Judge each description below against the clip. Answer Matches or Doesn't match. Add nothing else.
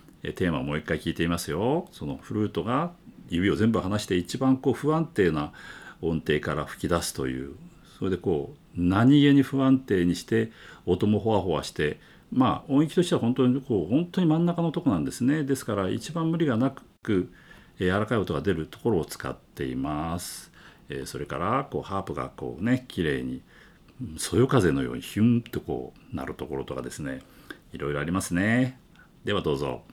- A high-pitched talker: Doesn't match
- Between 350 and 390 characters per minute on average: Matches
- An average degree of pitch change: Doesn't match